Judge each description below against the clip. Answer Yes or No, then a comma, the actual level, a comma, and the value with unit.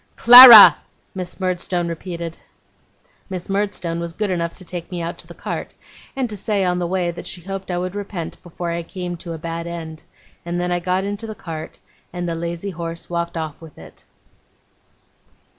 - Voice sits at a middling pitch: Yes, medium, 175 Hz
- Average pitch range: No, narrow, 2.1 semitones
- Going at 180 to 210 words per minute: Yes, average, 190 wpm